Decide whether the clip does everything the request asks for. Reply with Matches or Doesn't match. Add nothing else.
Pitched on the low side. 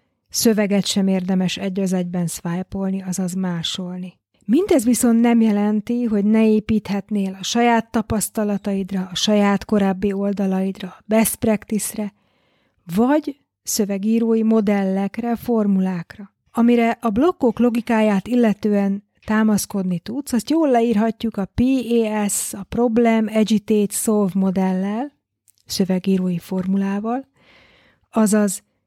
Doesn't match